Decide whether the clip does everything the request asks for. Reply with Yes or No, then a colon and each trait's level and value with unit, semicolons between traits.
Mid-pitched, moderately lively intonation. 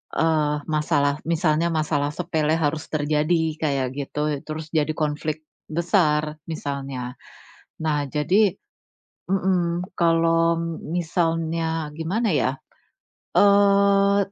No: medium, 160 Hz; narrow, 2.3 semitones